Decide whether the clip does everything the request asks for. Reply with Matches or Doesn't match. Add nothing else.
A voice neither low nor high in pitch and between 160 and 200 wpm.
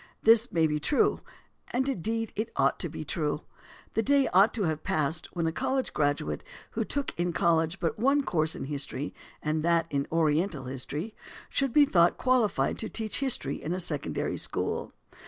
Matches